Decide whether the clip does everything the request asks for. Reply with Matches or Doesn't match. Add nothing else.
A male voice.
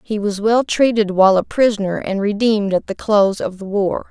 Doesn't match